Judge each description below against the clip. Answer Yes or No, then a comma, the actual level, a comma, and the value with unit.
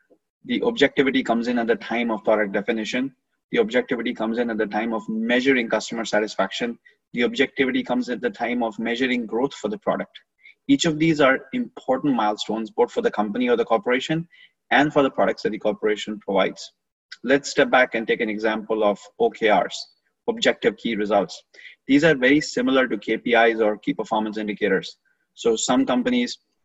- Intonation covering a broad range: No, average, 4.3 semitones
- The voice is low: Yes, low, 120 Hz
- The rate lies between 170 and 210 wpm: Yes, average, 180 wpm